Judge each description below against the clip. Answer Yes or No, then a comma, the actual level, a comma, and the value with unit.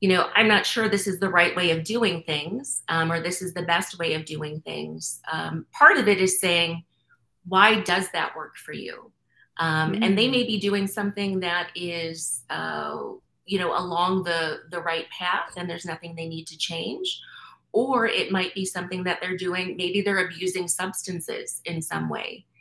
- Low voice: No, medium, 180 Hz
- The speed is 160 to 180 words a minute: No, average, 195 wpm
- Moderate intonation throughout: Yes, average, 3.1 semitones